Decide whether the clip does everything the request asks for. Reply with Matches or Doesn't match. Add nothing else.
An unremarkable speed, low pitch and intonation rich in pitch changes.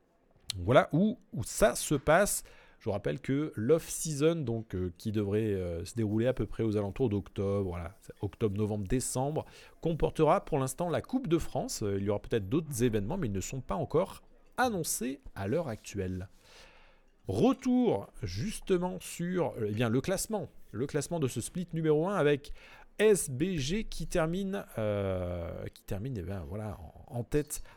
Matches